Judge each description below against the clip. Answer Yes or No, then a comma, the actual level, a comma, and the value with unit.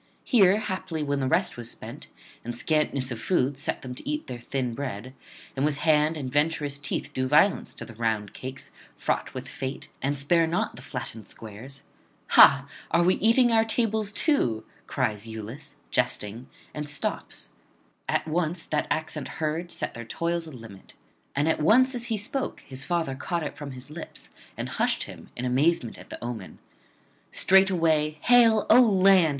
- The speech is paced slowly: No, average, 175 wpm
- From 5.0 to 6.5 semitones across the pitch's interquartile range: Yes, wide, 5.6 semitones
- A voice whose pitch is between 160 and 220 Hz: No, medium, 150 Hz